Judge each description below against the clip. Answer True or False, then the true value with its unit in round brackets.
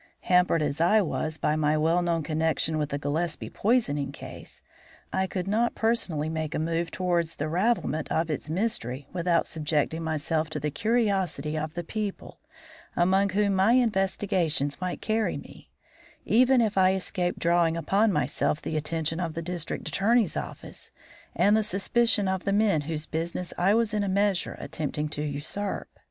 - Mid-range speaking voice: True (175 Hz)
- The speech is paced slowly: False (170 wpm)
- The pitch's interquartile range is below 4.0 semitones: False (4.3 semitones)